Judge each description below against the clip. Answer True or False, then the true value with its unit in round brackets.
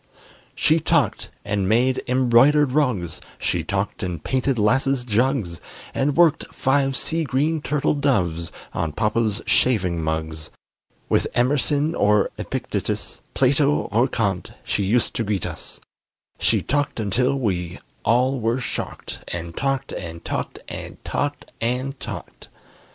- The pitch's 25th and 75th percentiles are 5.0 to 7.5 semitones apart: True (5.6 semitones)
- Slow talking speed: True (130 wpm)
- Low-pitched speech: True (125 Hz)